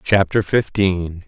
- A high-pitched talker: No, very low, 95 Hz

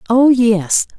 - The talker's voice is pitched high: Yes, high, 230 Hz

